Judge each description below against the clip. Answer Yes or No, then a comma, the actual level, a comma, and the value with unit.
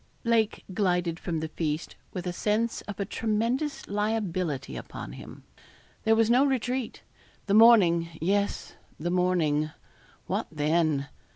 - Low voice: No, high, 190 Hz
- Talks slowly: Yes, slow, 130 wpm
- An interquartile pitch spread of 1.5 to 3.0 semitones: No, average, 5.0 semitones